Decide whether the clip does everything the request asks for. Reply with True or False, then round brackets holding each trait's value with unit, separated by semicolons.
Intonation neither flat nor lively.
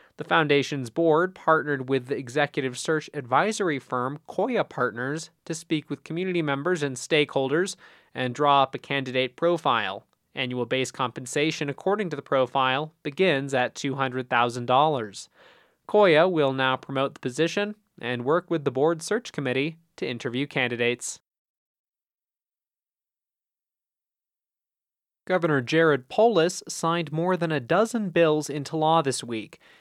True (3.9 semitones)